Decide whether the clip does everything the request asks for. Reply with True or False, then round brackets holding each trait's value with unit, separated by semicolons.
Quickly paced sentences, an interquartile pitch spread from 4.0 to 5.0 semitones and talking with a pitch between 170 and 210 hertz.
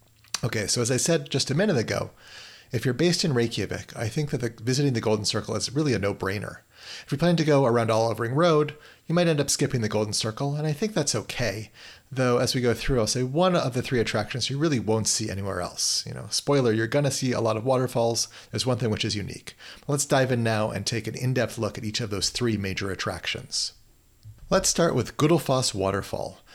False (235 wpm; 4.3 semitones; 120 Hz)